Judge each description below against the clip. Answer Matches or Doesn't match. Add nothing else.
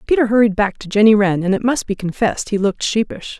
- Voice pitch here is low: Doesn't match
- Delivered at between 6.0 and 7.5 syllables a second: Matches